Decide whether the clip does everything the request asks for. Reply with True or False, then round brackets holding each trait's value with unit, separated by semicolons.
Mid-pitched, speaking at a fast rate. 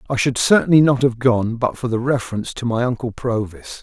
False (120 Hz; 220 wpm)